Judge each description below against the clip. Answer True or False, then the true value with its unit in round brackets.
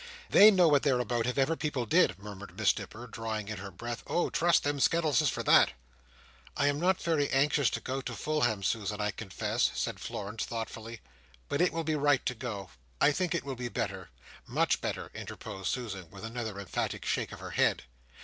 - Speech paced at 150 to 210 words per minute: True (200 wpm)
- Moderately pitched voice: False (125 Hz)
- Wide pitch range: True (5.7 semitones)